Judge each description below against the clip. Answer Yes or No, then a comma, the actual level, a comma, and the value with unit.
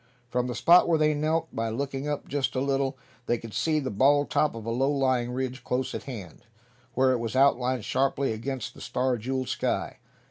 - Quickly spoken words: Yes, fast, 210 wpm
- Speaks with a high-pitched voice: No, low, 130 Hz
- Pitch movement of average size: No, narrow, 2.2 semitones